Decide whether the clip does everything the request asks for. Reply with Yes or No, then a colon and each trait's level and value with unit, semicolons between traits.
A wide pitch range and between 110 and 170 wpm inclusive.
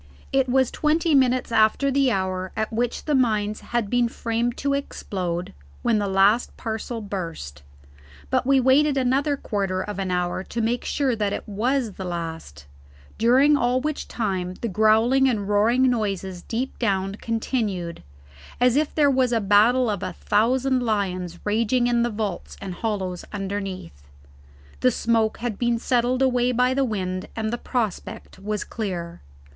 No: average, 4.3 semitones; average, 160 wpm